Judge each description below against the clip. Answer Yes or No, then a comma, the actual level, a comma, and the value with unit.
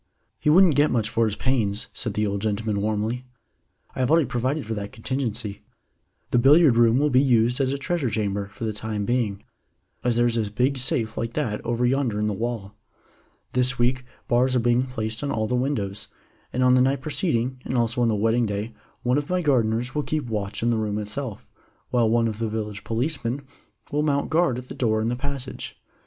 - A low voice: Yes, low, 120 Hz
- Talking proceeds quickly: Yes, fast, 215 wpm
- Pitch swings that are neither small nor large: Yes, average, 3.1 semitones